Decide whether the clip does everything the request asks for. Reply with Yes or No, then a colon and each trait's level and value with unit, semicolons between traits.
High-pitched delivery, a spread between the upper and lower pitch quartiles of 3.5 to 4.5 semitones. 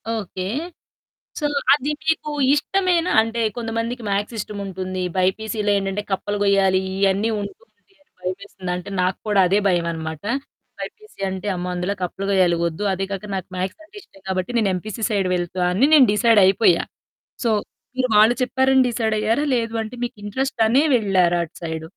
Yes: high, 200 Hz; average, 3.9 semitones